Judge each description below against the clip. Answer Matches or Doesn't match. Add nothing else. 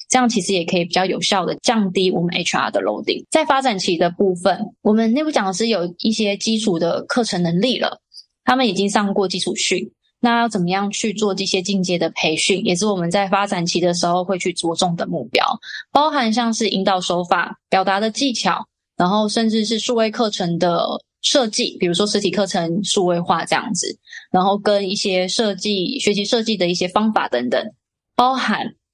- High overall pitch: Matches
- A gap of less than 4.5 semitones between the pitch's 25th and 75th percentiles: Matches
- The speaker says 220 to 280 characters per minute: Doesn't match